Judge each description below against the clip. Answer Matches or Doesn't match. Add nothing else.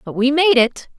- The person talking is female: Matches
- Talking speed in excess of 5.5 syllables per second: Doesn't match